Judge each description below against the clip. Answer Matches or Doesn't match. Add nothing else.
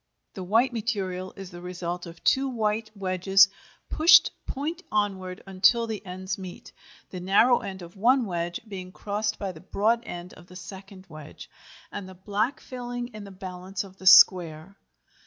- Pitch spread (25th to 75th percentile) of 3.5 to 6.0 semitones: Doesn't match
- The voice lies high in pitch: Matches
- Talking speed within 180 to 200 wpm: Doesn't match